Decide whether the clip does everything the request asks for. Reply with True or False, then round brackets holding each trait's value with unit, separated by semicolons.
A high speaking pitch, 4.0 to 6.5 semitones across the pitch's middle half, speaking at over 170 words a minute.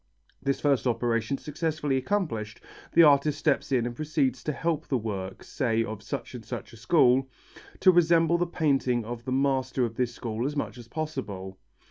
False (130 Hz; 4.6 semitones; 180 wpm)